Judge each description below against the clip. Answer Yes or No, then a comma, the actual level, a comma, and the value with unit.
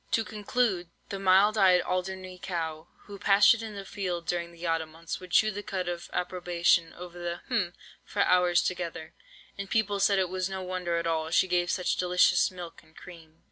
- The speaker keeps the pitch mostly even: Yes, narrow, 2.1 semitones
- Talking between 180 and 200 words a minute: Yes, average, 190 wpm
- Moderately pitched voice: Yes, medium, 180 Hz